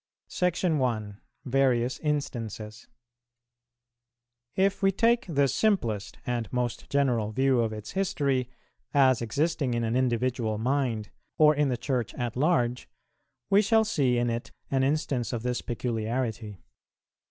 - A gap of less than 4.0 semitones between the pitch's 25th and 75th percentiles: Yes, average, 3.6 semitones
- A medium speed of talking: No, slow, 130 wpm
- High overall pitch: No, low, 125 Hz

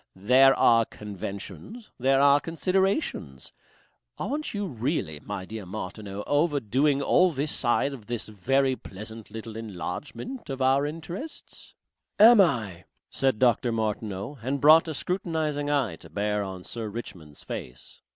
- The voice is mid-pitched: No, low, 125 Hz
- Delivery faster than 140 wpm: No, slow, 135 wpm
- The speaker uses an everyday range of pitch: No, wide, 6.2 semitones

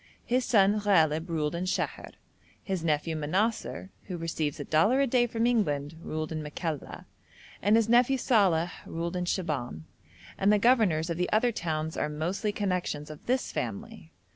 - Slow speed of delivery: No, average, 165 wpm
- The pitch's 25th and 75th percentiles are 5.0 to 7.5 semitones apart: Yes, average, 5.3 semitones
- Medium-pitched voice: Yes, medium, 180 Hz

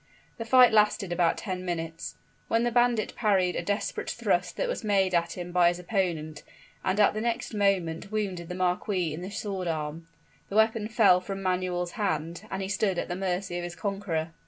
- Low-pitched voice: No, medium, 185 Hz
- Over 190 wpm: Yes, average, 200 wpm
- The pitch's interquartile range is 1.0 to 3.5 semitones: Yes, average, 3.2 semitones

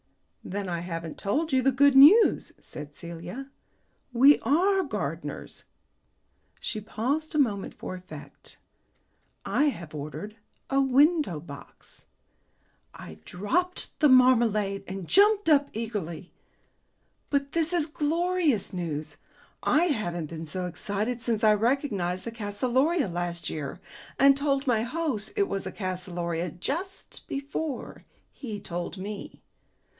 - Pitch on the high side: Yes, high, 230 Hz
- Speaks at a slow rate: Yes, slow, 125 wpm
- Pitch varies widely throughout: Yes, wide, 8.0 semitones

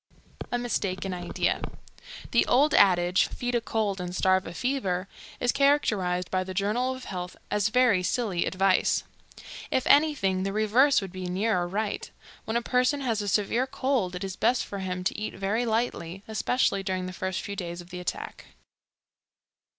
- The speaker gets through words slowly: No, average, 175 wpm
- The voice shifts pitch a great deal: No, average, 4.8 semitones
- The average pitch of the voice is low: No, high, 200 Hz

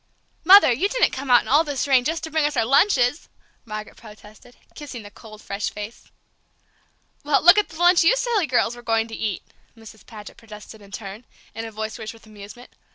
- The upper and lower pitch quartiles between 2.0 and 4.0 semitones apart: No, wide, 5.5 semitones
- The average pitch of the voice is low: No, high, 240 Hz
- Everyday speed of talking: No, fast, 210 wpm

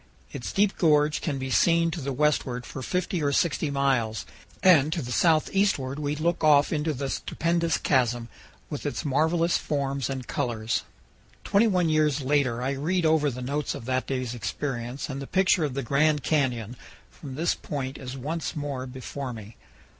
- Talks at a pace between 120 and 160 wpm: No, average, 175 wpm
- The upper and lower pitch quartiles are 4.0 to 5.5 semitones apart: No, average, 3.5 semitones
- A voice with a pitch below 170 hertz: Yes, medium, 140 Hz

